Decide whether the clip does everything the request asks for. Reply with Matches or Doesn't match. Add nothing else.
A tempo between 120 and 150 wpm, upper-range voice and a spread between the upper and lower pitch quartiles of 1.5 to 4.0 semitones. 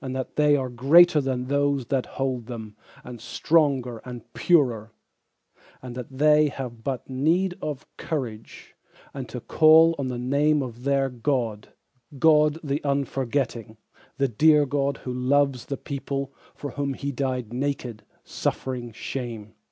Doesn't match